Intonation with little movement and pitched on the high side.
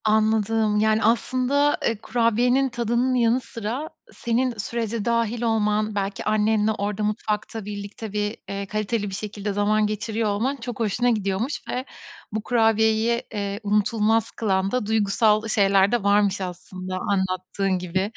Yes: narrow, 2.2 semitones; high, 215 Hz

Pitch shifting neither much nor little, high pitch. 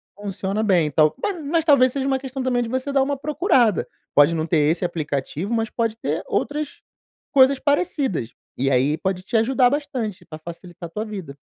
No: wide, 8.2 semitones; high, 220 Hz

